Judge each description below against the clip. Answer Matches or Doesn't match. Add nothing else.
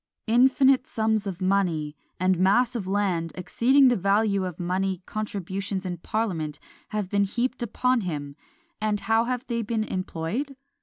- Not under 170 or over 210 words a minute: Doesn't match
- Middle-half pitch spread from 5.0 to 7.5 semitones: Doesn't match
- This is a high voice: Matches